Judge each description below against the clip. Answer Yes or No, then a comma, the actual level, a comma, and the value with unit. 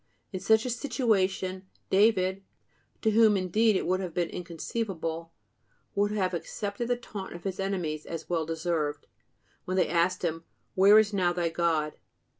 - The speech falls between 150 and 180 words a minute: Yes, average, 160 wpm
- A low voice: No, medium, 185 Hz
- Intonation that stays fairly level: No, average, 3.4 semitones